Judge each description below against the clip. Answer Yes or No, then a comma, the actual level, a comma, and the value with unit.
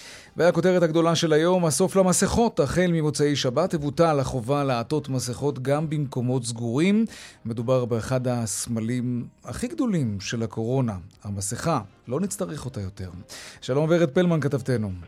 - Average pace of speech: Yes, average, 125 wpm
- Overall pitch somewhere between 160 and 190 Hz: No, low, 135 Hz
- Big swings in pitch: Yes, wide, 5.9 semitones